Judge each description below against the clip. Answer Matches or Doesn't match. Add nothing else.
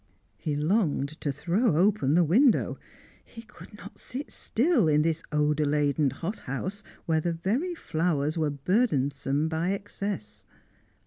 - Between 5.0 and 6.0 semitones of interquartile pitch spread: Matches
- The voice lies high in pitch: Doesn't match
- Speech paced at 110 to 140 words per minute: Matches